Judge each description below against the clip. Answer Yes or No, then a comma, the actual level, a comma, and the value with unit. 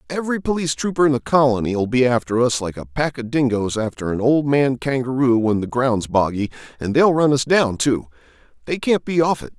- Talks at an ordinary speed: No, fast, 215 wpm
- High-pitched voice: No, low, 130 Hz